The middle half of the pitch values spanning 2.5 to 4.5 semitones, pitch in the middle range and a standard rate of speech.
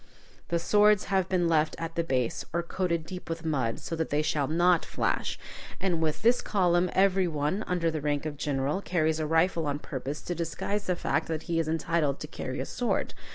No: average, 3.0 semitones; medium, 165 Hz; fast, 210 wpm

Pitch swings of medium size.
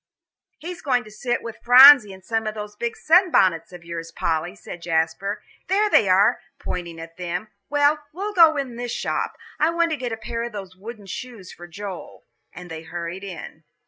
No: wide, 6.2 semitones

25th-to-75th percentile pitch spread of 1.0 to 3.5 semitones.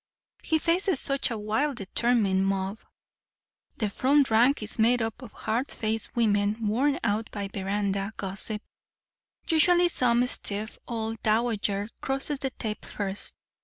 No: average, 4.0 semitones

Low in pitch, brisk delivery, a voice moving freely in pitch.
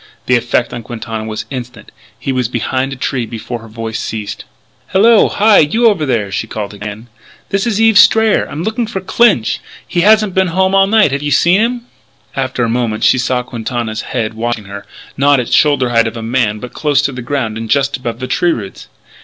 Yes: low, 125 Hz; fast, 215 wpm; wide, 7.7 semitones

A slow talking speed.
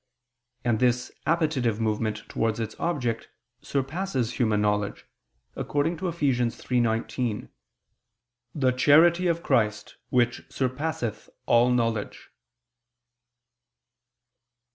Yes: slow, 90 wpm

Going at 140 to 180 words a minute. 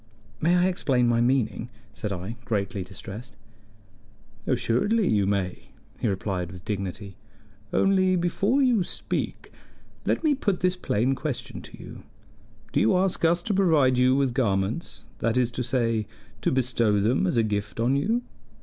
Yes: average, 160 wpm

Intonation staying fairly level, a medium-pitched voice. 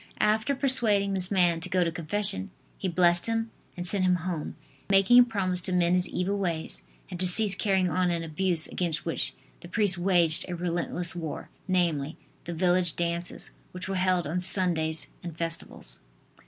Yes: narrow, 2.1 semitones; medium, 180 Hz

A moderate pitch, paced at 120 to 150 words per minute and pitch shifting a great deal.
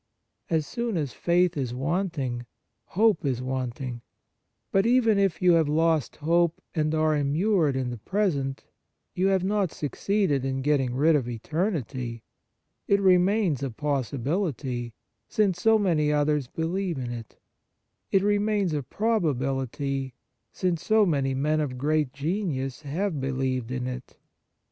Yes: medium, 150 Hz; average, 140 wpm; wide, 5.8 semitones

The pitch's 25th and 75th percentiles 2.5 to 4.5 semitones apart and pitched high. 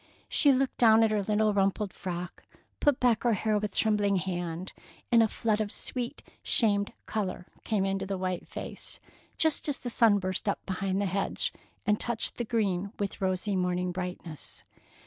Yes: average, 2.9 semitones; high, 205 Hz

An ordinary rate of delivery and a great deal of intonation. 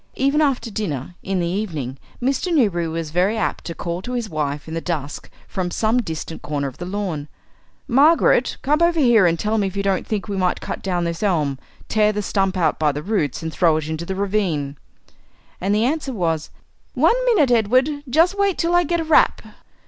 No: fast, 210 wpm; wide, 7.0 semitones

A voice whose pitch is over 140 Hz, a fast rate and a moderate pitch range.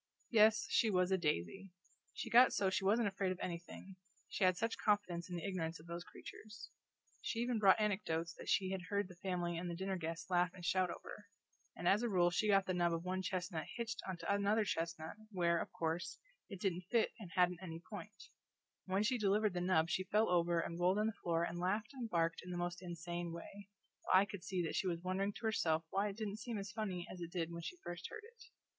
Yes: medium, 185 Hz; fast, 235 wpm; average, 3.1 semitones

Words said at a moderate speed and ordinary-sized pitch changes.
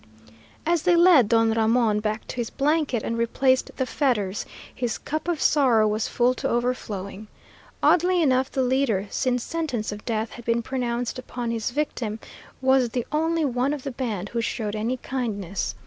Yes: average, 175 wpm; average, 3.4 semitones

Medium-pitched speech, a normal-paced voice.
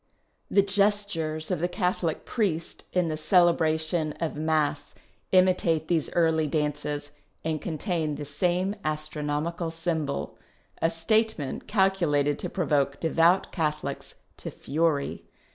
No: medium, 160 Hz; slow, 120 wpm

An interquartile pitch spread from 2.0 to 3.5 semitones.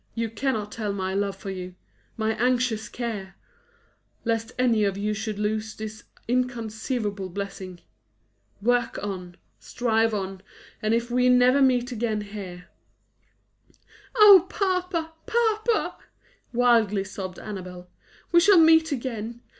No: average, 3.9 semitones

